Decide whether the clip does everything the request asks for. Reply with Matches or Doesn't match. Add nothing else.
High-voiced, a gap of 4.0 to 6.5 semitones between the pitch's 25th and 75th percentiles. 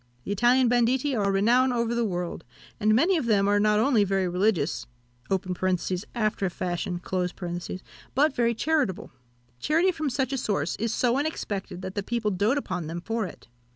Matches